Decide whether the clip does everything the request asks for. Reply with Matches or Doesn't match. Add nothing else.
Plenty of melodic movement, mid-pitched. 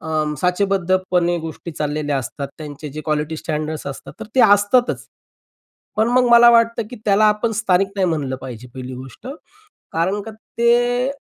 Matches